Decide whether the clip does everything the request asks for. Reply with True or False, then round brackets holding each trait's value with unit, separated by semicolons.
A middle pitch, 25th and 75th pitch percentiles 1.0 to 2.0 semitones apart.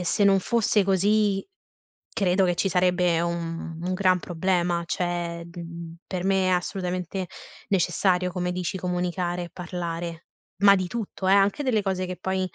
True (180 Hz; 1.7 semitones)